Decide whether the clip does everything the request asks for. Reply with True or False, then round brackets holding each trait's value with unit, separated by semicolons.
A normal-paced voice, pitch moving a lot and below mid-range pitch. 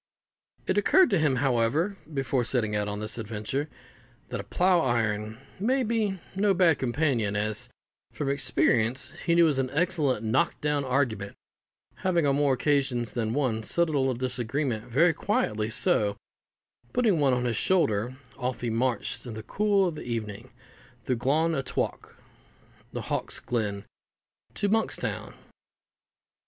True (155 wpm; 6.2 semitones; 130 Hz)